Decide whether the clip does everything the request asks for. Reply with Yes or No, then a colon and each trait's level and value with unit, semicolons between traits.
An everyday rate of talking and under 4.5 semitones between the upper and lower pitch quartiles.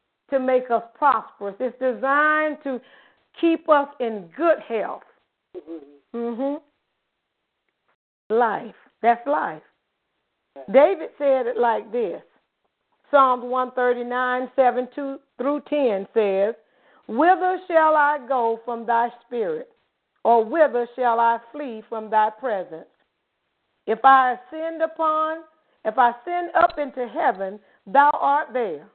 No: slow, 120 wpm; average, 4.1 semitones